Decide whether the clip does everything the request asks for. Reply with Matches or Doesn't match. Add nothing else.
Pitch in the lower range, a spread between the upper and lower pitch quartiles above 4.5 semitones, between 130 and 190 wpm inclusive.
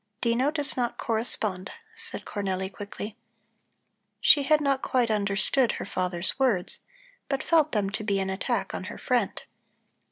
Doesn't match